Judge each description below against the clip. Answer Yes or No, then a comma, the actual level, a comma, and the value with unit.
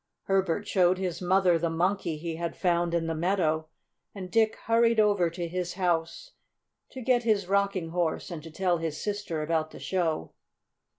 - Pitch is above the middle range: No, medium, 175 Hz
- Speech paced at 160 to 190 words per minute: Yes, average, 175 wpm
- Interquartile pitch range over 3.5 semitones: No, average, 3.2 semitones